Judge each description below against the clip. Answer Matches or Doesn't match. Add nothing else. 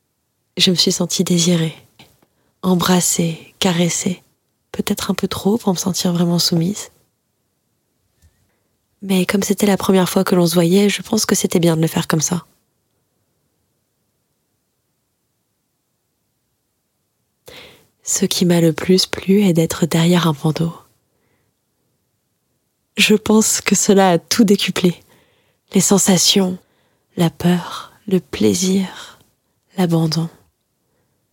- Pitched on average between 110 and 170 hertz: Doesn't match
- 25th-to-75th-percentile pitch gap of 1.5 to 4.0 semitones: Matches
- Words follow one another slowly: Matches